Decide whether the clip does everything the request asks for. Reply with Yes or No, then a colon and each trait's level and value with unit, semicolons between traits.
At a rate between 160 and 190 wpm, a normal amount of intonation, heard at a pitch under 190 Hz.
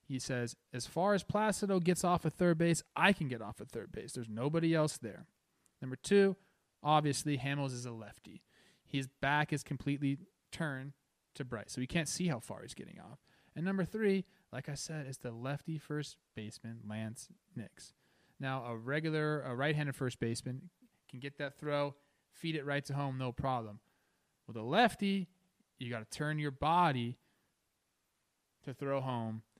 Yes: average, 180 wpm; average, 4.7 semitones; medium, 140 Hz